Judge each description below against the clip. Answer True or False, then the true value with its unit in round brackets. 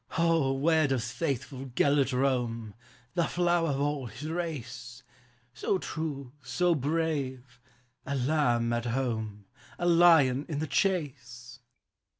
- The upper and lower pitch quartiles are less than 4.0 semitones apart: False (4.5 semitones)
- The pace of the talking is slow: True (130 wpm)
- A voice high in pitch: False (135 Hz)